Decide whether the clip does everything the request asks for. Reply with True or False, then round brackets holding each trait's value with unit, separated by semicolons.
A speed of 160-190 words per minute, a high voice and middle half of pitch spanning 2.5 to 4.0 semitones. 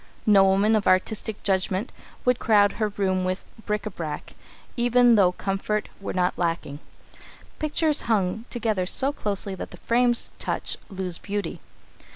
False (150 wpm; 205 Hz; 3.2 semitones)